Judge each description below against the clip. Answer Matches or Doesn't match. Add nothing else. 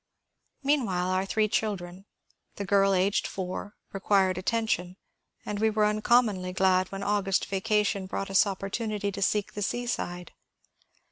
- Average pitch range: Doesn't match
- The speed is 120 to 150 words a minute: Matches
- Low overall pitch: Doesn't match